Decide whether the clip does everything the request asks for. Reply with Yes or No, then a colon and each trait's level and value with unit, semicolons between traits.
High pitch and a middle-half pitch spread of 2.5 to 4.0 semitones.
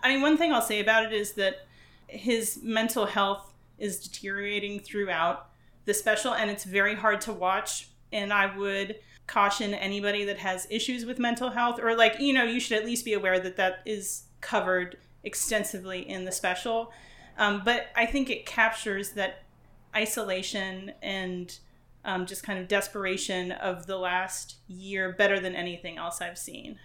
Yes: high, 205 Hz; average, 2.9 semitones